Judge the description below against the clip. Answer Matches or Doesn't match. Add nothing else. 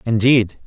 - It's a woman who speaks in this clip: Doesn't match